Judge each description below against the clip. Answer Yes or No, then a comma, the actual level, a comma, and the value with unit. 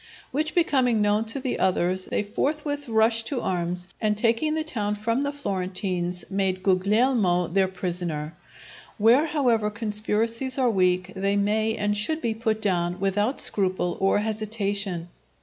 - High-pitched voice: Yes, high, 210 Hz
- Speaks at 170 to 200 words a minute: No, average, 150 wpm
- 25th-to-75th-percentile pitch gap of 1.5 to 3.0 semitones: No, average, 3.7 semitones